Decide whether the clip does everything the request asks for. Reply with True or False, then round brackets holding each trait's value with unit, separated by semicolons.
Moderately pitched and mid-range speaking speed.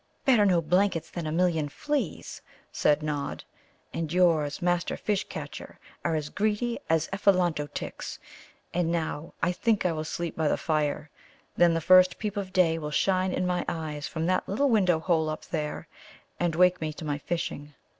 True (170 Hz; 180 wpm)